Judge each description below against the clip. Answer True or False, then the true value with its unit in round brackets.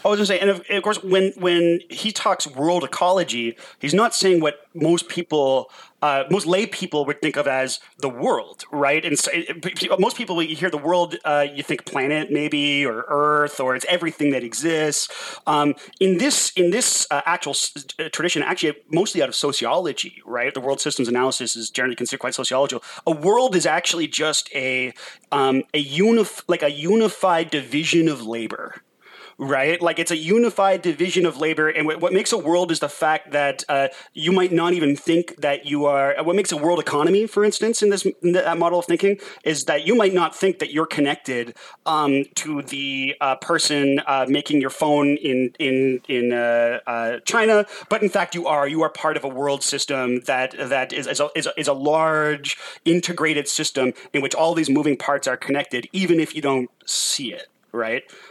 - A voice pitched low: False (155 Hz)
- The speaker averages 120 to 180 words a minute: False (200 wpm)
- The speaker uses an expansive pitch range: False (4.0 semitones)